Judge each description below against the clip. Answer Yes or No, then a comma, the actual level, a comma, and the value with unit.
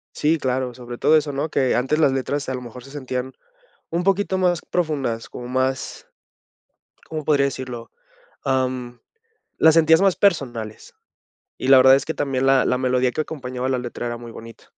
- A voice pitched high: No, low, 130 Hz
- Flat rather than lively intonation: No, average, 3.3 semitones